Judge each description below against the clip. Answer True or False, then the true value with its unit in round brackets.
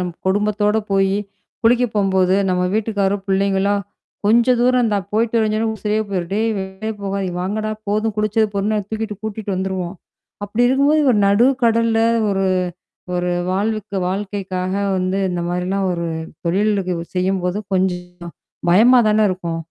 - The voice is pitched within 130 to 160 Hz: False (200 Hz)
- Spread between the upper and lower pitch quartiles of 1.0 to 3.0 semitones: True (2.5 semitones)